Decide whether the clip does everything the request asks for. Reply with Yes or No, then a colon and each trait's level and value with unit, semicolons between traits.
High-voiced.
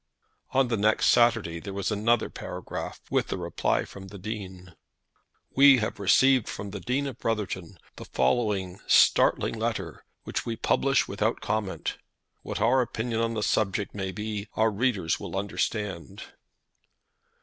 No: low, 105 Hz